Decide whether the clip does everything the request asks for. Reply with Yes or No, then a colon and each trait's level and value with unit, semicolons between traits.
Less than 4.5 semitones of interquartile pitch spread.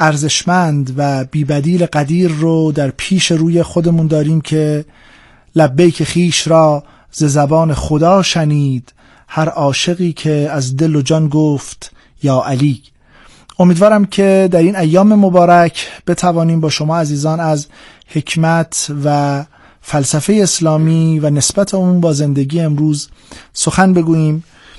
Yes: narrow, 2.6 semitones